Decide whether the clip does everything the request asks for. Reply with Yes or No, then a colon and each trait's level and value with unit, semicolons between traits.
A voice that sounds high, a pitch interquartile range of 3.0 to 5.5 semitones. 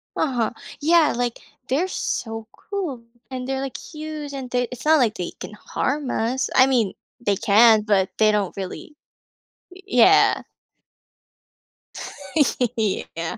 Yes: very high, 250 Hz; average, 5.1 semitones